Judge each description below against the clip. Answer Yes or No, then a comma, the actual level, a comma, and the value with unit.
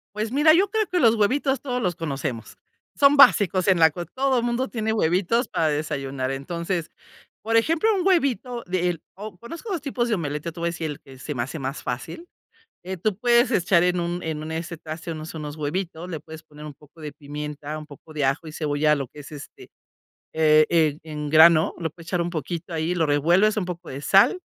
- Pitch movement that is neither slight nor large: No, wide, 6.2 semitones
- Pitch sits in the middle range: Yes, medium, 170 Hz